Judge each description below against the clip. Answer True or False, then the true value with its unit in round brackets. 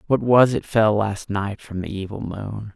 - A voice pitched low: True (105 Hz)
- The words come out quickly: True (220 wpm)